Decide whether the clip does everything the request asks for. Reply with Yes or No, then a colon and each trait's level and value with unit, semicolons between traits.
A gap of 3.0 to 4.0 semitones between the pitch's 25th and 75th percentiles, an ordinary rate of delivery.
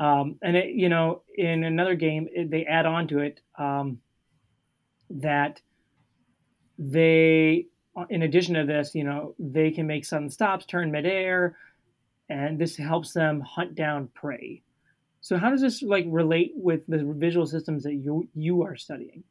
No: narrow, 2.6 semitones; average, 160 wpm